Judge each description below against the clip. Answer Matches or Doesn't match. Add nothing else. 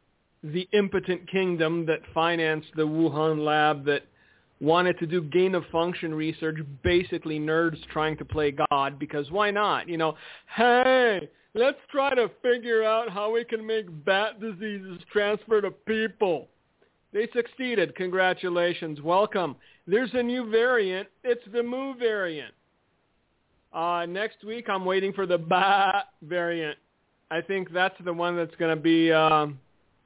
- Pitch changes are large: Doesn't match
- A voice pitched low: Doesn't match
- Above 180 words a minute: Doesn't match